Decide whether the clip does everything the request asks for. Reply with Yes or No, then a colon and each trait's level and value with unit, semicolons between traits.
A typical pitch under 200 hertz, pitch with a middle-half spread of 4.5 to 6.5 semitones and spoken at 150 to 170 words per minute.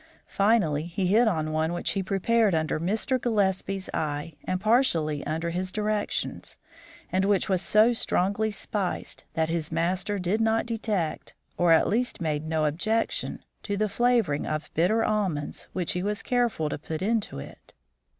Yes: high, 190 Hz; average, 5.0 semitones; average, 160 wpm